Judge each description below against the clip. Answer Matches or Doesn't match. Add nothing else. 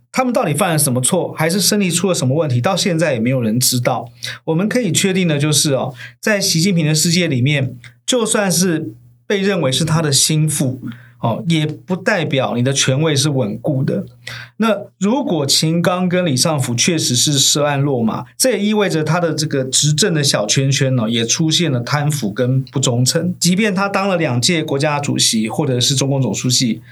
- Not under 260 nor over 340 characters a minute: Matches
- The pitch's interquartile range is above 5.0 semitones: Matches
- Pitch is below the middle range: Doesn't match